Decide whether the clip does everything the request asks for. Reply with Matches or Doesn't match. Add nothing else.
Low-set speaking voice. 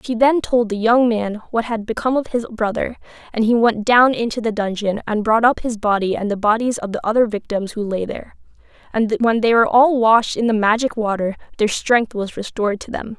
Doesn't match